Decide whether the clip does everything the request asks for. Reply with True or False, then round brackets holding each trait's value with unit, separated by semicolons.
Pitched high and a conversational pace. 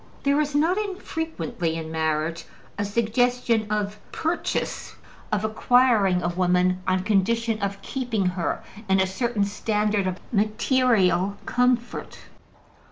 False (210 Hz; 120 wpm)